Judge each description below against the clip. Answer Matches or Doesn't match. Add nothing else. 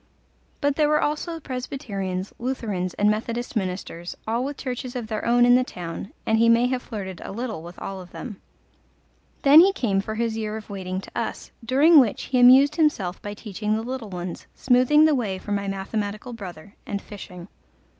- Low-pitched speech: Doesn't match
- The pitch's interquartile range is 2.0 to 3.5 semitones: Doesn't match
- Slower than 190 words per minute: Doesn't match